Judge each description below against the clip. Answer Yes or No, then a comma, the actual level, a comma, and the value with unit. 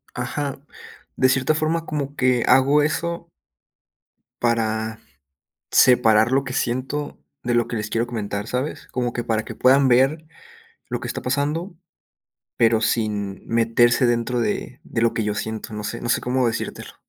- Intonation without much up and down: No, average, 3.3 semitones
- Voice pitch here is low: Yes, low, 120 Hz